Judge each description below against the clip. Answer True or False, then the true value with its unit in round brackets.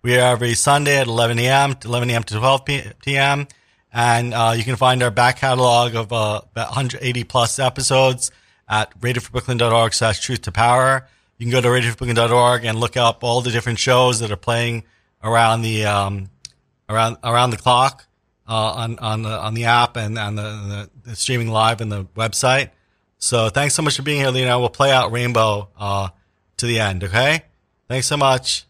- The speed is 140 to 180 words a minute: False (190 wpm)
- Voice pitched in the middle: False (120 Hz)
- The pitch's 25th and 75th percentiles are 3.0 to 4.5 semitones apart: False (2.5 semitones)